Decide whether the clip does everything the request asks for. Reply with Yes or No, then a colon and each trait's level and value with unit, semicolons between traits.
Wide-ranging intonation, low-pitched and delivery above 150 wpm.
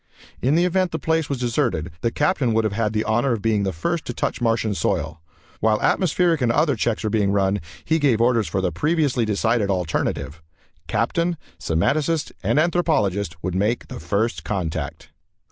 Yes: wide, 6.9 semitones; low, 115 Hz; average, 180 wpm